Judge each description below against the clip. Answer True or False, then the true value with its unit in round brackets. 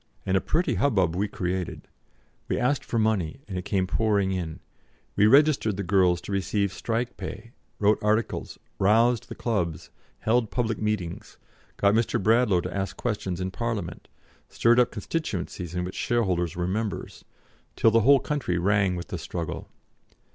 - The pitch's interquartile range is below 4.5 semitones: True (3.9 semitones)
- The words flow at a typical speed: True (160 wpm)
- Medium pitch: False (100 Hz)